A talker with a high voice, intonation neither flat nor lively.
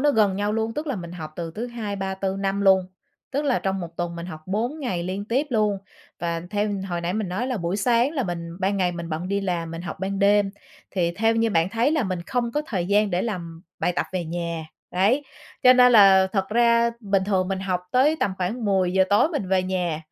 Yes: high, 195 Hz; average, 4.1 semitones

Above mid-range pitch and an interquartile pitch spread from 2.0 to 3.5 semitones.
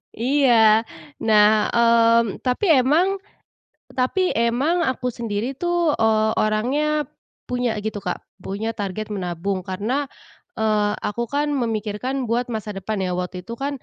Yes: high, 225 Hz; average, 3.2 semitones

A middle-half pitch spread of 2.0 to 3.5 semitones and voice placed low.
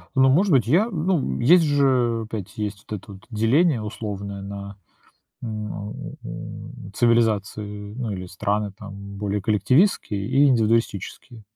No: average, 4.3 semitones; low, 110 Hz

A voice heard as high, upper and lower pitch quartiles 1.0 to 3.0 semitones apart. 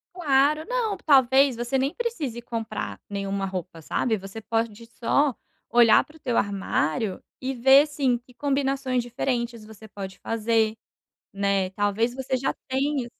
No: high, 240 Hz; average, 4.2 semitones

